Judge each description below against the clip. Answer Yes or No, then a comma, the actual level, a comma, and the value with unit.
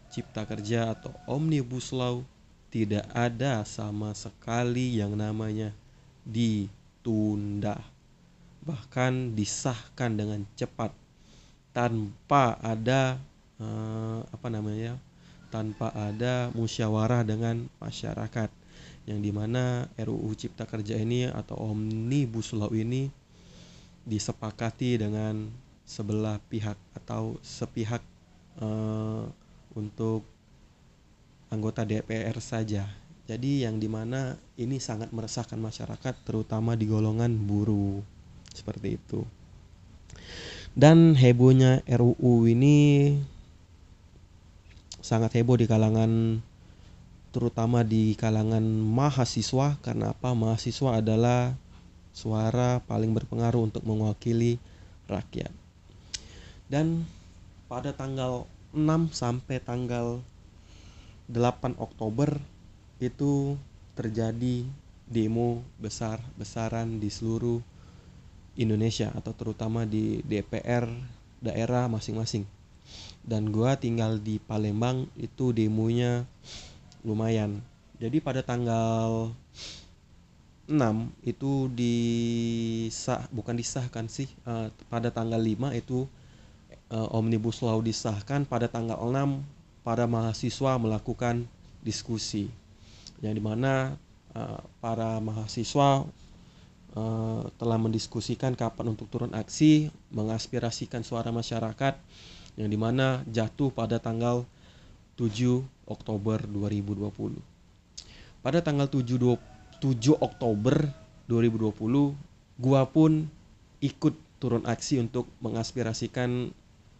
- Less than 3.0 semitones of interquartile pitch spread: Yes, narrow, 2.5 semitones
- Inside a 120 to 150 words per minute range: No, average, 90 wpm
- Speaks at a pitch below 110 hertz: No, low, 115 Hz